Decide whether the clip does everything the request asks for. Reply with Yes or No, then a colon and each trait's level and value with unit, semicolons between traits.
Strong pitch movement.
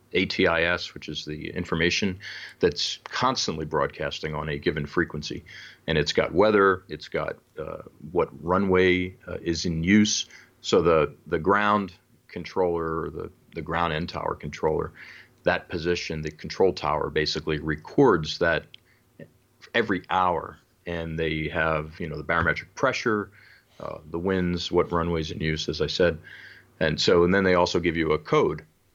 No: average, 3.1 semitones